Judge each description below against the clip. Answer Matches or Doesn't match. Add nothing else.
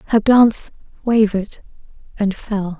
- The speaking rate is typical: Doesn't match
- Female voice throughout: Matches